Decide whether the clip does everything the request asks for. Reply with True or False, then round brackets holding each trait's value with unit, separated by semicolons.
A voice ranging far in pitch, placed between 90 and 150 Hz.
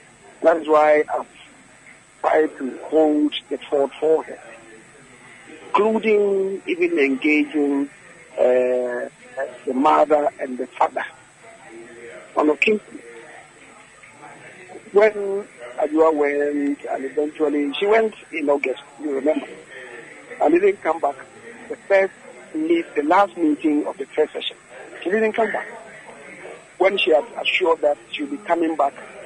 False (7.1 semitones; 160 Hz)